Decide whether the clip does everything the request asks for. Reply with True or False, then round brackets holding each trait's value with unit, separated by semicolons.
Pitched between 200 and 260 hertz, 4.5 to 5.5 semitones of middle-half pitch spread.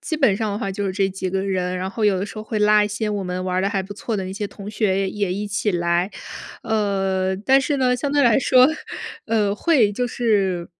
False (205 Hz; 2.5 semitones)